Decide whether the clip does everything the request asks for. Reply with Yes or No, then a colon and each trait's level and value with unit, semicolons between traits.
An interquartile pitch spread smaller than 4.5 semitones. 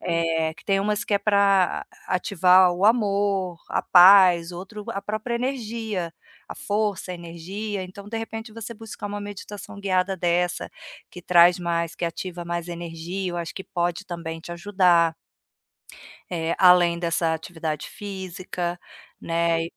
Yes: average, 3.0 semitones